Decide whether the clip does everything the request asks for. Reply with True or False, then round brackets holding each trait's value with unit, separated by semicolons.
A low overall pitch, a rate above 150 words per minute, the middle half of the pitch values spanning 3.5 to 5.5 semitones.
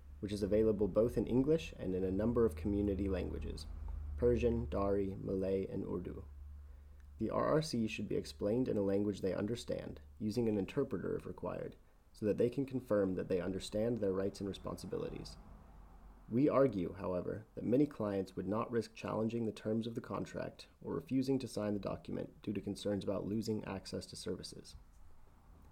True (100 Hz; 175 wpm; 4.0 semitones)